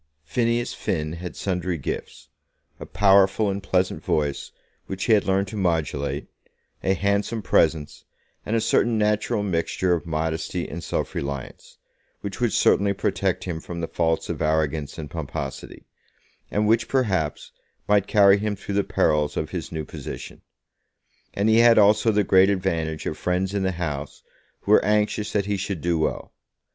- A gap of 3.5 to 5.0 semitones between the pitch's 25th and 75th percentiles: Yes, average, 4.3 semitones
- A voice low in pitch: Yes, very low, 95 Hz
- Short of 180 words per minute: Yes, average, 165 wpm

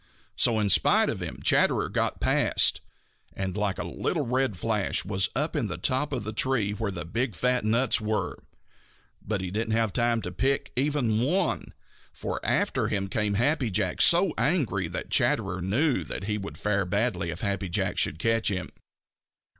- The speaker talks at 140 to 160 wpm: No, average, 180 wpm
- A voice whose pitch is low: Yes, low, 110 Hz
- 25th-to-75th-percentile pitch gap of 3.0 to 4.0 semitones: No, average, 4.4 semitones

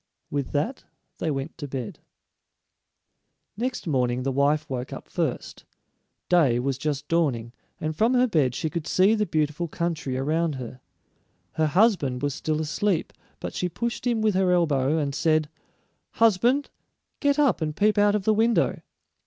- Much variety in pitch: Yes, wide, 6.7 semitones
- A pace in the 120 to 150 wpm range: No, average, 160 wpm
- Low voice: No, medium, 155 Hz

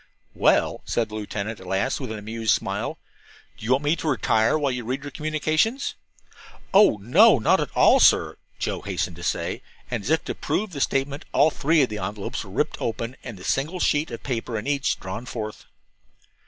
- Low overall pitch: Yes, low, 125 Hz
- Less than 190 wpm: No, average, 195 wpm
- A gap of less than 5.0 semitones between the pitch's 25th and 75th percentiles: No, wide, 5.5 semitones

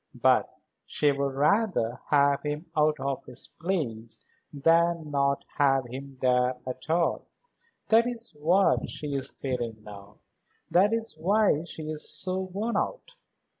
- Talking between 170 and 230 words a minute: No, average, 140 wpm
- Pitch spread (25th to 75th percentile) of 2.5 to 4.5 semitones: No, average, 5.2 semitones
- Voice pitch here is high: No, medium, 150 Hz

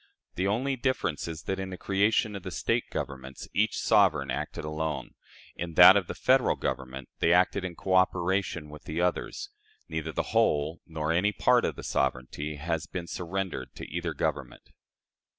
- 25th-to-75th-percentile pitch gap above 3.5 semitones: Yes, average, 4.1 semitones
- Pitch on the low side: Yes, very low, 85 Hz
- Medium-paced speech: Yes, average, 170 wpm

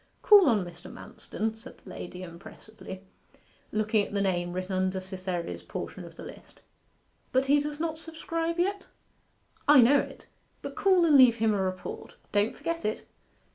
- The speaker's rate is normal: Yes, average, 170 wpm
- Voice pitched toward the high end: Yes, high, 220 Hz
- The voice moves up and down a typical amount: No, wide, 8.1 semitones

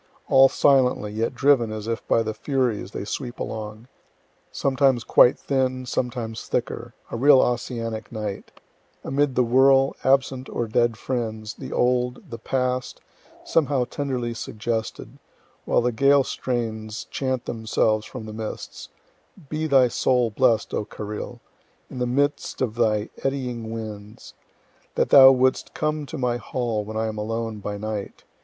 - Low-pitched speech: Yes, low, 120 Hz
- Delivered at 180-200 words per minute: No, average, 150 wpm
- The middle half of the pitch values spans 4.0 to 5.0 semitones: No, average, 3.1 semitones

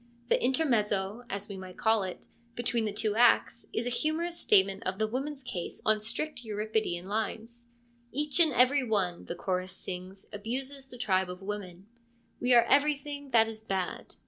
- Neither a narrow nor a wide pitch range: Yes, average, 4.8 semitones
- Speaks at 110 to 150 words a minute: No, average, 170 wpm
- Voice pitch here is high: Yes, high, 220 Hz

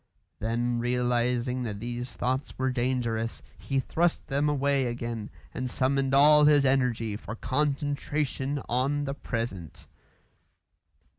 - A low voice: Yes, low, 130 Hz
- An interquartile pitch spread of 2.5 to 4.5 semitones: Yes, average, 2.8 semitones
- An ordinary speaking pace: No, slow, 120 wpm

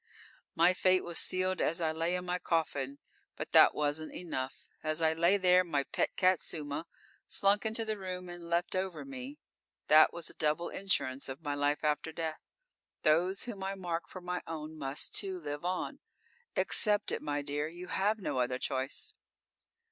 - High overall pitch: No, medium, 170 Hz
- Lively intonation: No, average, 3.5 semitones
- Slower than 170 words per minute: No, average, 180 wpm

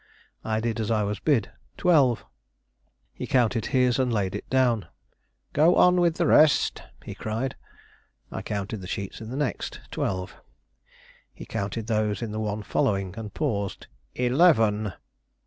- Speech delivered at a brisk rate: No, average, 150 wpm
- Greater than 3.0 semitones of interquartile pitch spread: Yes, average, 4.1 semitones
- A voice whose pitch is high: No, low, 110 Hz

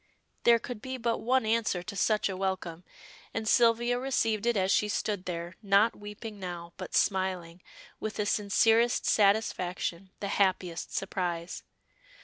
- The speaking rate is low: No, average, 145 wpm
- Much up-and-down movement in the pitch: No, average, 3.4 semitones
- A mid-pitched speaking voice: No, high, 200 Hz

